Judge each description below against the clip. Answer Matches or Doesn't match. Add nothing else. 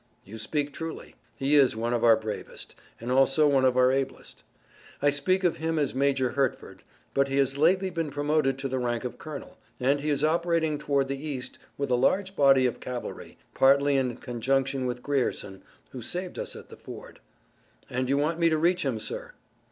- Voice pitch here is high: Doesn't match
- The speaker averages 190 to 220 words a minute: Matches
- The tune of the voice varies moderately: Matches